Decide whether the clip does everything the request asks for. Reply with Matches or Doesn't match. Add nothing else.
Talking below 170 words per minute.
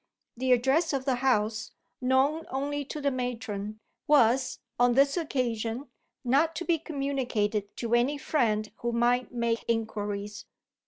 Matches